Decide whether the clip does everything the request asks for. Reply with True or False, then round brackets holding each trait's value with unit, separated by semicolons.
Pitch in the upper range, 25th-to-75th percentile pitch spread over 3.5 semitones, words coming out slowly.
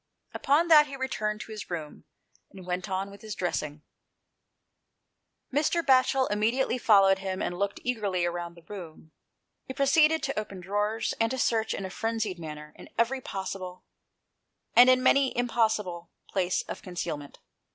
False (205 Hz; 5.5 semitones; 170 wpm)